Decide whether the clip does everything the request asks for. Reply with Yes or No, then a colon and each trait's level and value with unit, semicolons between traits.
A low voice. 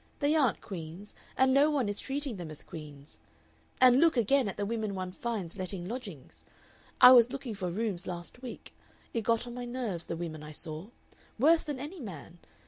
No: high, 220 Hz